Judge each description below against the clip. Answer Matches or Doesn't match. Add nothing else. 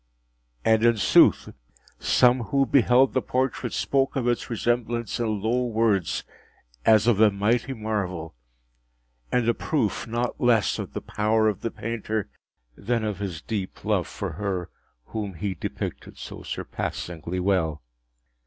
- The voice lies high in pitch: Doesn't match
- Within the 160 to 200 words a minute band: Doesn't match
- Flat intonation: Doesn't match